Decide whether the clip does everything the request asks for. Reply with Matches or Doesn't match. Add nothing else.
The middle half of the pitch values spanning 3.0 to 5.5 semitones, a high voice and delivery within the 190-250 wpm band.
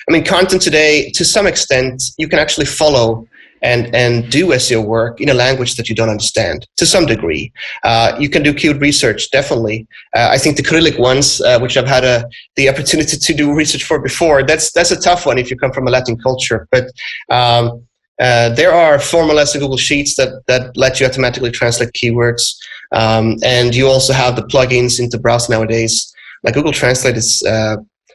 Doesn't match